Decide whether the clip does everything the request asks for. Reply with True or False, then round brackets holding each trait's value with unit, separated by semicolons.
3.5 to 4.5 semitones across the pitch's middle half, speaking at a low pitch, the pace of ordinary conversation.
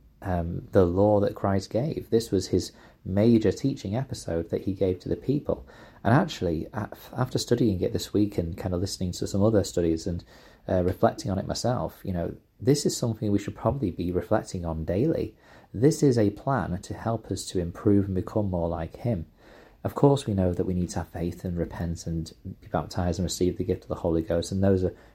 False (3.8 semitones; 95 Hz; 215 wpm)